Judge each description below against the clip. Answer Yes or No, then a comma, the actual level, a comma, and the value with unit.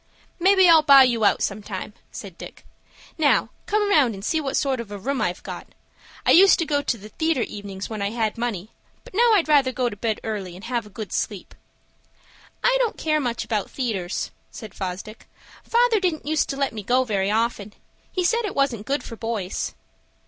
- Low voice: No, high, 240 Hz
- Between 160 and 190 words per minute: No, fast, 205 wpm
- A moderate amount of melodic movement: No, wide, 6.7 semitones